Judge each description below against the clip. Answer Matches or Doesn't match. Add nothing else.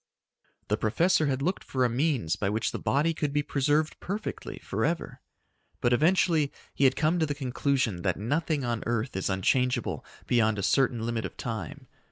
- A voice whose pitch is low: Matches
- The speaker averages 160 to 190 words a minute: Matches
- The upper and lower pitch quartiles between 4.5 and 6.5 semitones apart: Matches